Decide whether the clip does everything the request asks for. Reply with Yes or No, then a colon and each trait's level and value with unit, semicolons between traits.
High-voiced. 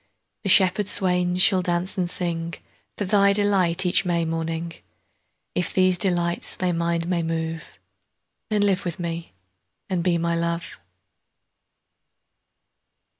No: medium, 175 Hz